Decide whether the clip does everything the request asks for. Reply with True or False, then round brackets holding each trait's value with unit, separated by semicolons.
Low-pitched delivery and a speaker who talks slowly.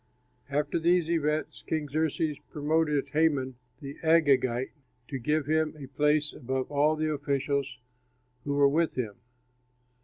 False (150 Hz; 130 wpm)